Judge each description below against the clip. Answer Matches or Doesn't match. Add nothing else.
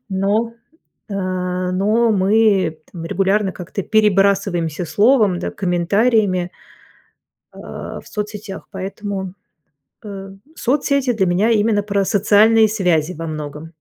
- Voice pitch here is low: Doesn't match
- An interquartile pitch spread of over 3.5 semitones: Doesn't match